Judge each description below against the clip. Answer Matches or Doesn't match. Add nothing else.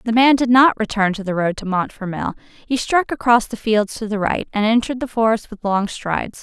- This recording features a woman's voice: Matches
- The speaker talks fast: Matches